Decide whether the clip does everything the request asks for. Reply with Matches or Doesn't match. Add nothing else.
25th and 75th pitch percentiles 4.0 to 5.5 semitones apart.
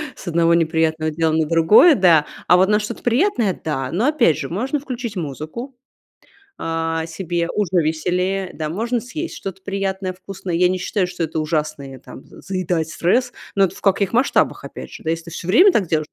Matches